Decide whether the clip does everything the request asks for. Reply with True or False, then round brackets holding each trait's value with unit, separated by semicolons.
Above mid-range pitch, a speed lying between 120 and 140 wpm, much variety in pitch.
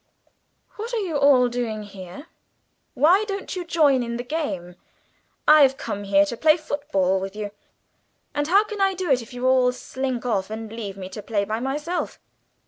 False (250 Hz; 180 wpm; 6.6 semitones)